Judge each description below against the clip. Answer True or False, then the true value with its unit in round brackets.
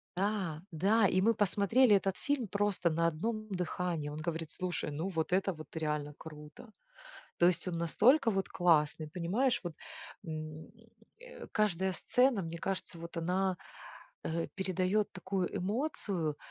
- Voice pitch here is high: False (180 Hz)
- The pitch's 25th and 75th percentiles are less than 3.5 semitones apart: False (3.9 semitones)